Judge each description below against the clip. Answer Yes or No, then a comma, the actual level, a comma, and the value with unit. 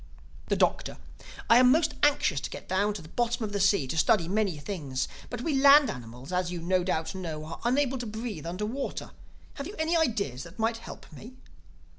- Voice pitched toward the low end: No, high, 205 Hz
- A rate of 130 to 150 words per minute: No, fast, 205 wpm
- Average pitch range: No, wide, 7.0 semitones